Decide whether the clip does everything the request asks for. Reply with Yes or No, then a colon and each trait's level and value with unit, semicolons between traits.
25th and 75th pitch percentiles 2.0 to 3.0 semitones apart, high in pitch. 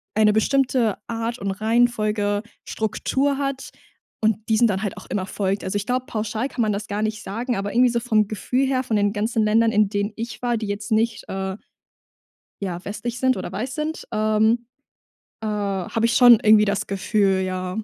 Yes: average, 2.7 semitones; high, 215 Hz